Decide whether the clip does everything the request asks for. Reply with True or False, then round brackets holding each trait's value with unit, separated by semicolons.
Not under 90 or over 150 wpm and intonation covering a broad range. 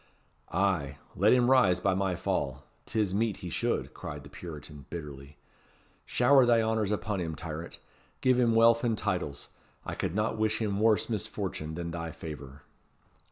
False (160 wpm; 6.3 semitones)